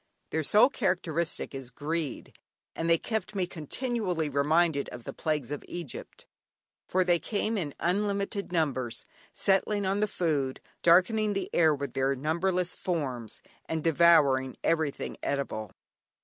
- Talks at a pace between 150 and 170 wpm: No, slow, 135 wpm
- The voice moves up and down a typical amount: Yes, average, 5.0 semitones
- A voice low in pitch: No, medium, 165 Hz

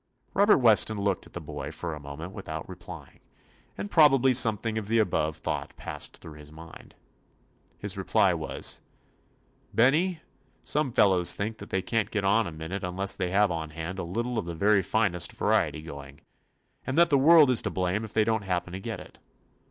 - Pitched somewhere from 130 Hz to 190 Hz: No, low, 100 Hz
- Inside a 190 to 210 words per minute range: Yes, average, 200 wpm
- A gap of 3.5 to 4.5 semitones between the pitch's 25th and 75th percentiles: No, average, 5.0 semitones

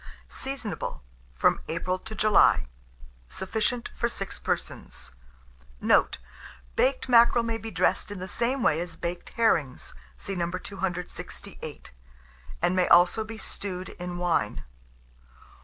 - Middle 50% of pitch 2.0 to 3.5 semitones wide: No, average, 4.3 semitones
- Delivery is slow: Yes, slow, 125 wpm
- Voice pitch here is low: No, high, 190 Hz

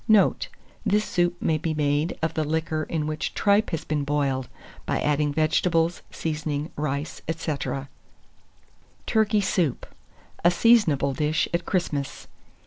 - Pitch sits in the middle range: Yes, medium, 155 Hz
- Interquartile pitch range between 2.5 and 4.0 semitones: Yes, average, 2.9 semitones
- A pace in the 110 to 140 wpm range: Yes, slow, 135 wpm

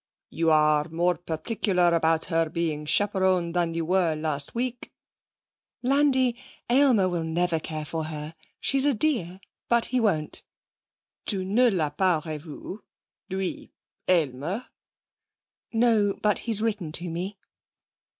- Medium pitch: Yes, medium, 180 Hz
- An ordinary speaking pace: No, slow, 130 wpm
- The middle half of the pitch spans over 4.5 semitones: Yes, average, 5.2 semitones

